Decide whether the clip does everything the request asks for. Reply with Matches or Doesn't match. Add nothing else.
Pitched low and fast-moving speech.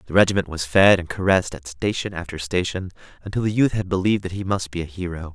Matches